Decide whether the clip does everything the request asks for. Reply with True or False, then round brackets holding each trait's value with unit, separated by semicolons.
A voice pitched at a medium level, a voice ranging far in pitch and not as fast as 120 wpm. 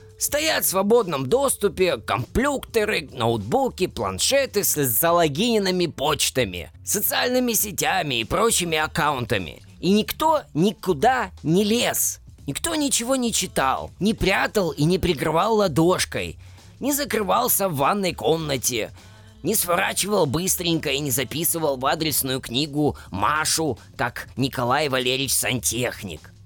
True (165 Hz; 8.3 semitones; 110 wpm)